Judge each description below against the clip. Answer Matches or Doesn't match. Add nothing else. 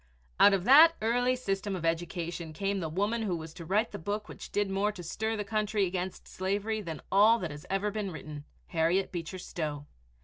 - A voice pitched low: Doesn't match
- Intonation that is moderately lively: Matches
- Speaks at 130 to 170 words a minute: Doesn't match